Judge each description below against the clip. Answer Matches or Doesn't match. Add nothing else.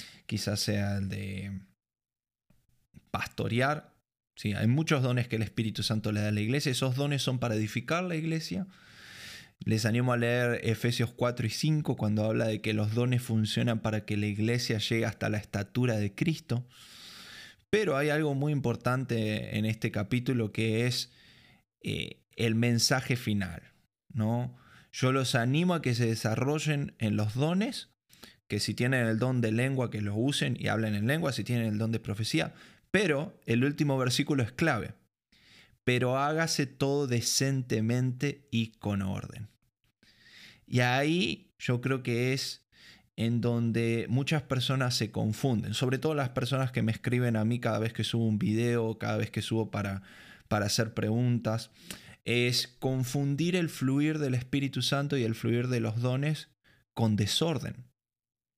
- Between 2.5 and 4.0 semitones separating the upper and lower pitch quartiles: Matches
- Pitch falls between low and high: Doesn't match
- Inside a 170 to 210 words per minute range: Doesn't match